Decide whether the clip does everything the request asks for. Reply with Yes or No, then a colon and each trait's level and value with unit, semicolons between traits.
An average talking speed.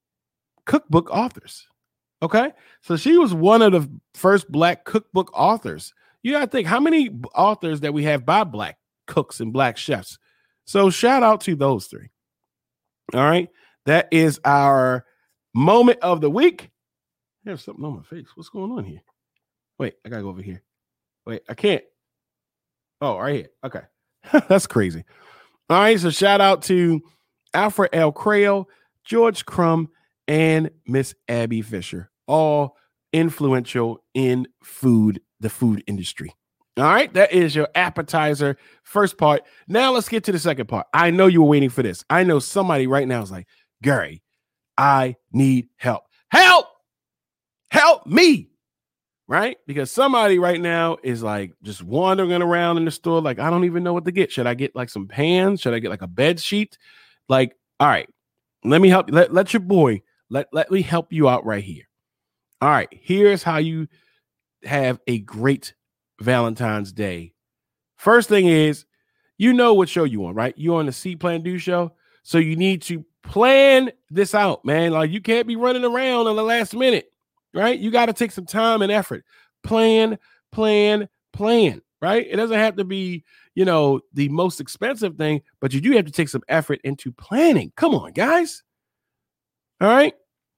Yes: average, 175 wpm